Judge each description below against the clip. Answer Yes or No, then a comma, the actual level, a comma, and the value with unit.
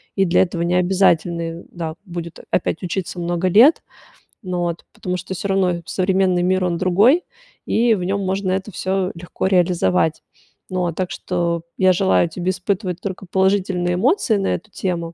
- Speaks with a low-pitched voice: No, medium, 185 Hz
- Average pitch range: No, narrow, 1.9 semitones